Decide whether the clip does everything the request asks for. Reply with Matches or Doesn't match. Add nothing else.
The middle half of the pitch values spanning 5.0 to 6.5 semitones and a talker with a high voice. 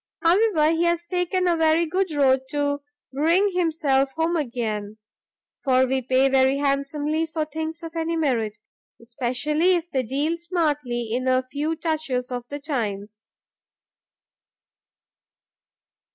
Doesn't match